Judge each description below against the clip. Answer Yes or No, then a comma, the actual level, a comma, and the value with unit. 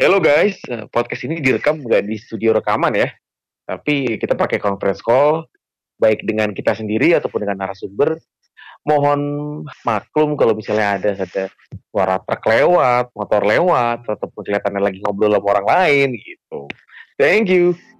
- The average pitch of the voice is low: Yes, low, 110 Hz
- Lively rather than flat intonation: Yes, wide, 5.9 semitones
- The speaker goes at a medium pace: No, fast, 145 wpm